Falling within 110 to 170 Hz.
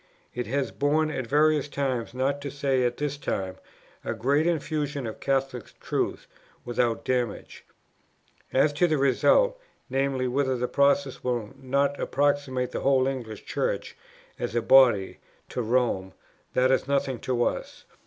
Yes: low, 135 Hz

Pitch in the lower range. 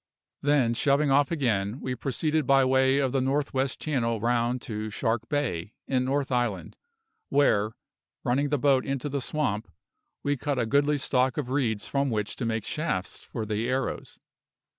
Yes: low, 130 Hz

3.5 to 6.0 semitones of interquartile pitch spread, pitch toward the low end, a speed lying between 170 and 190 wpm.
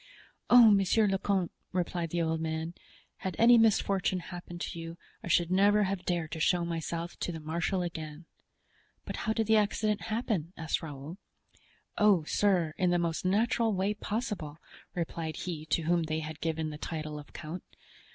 No: average, 3.8 semitones; medium, 175 Hz; average, 175 wpm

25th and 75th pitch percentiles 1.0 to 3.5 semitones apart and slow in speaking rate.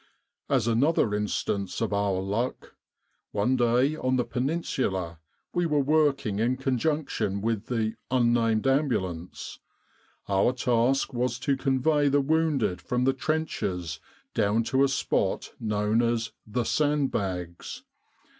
No: average, 4.7 semitones; slow, 125 wpm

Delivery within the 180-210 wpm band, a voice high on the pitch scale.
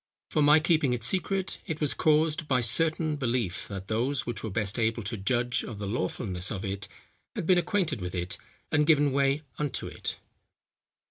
No: average, 185 wpm; low, 130 Hz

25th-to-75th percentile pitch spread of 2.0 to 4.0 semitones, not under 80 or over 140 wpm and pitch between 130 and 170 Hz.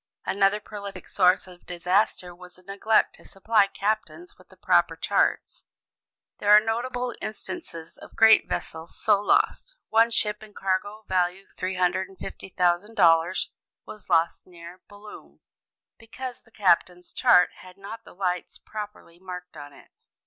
No: average, 3.2 semitones; slow, 135 wpm; high, 195 Hz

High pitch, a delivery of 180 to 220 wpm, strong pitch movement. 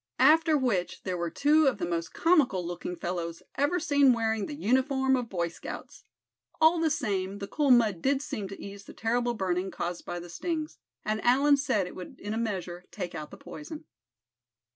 Yes: high, 225 Hz; average, 195 wpm; wide, 7.7 semitones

